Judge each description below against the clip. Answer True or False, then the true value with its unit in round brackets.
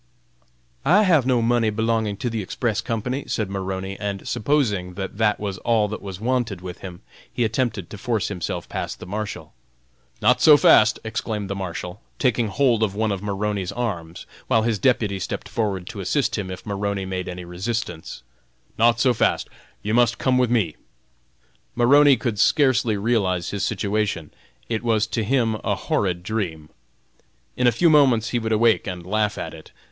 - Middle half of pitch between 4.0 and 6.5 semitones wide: False (3.5 semitones)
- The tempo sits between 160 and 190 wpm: True (175 wpm)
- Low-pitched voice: True (110 Hz)